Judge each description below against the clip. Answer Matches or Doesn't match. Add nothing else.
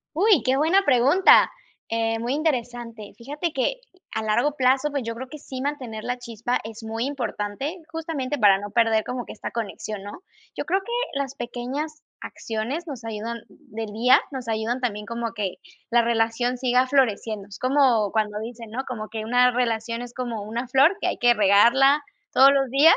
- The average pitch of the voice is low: Doesn't match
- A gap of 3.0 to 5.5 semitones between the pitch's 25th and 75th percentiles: Matches